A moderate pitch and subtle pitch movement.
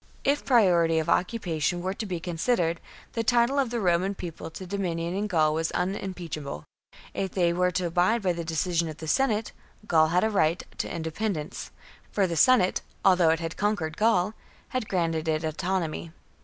No: medium, 180 Hz; average, 3.6 semitones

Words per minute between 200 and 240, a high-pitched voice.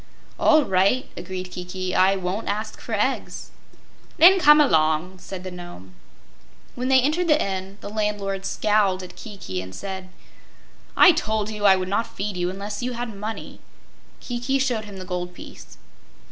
No: average, 165 wpm; high, 200 Hz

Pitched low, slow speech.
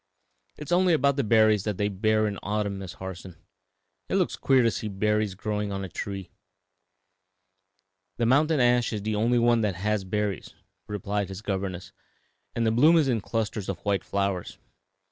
No: low, 105 Hz; average, 185 wpm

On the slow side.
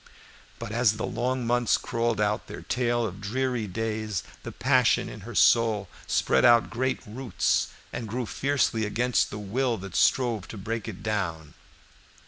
No: average, 160 wpm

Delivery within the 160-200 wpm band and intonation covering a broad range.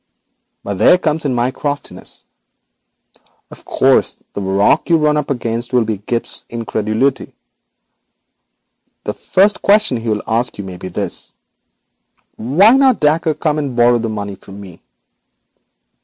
No: average, 145 wpm; wide, 5.9 semitones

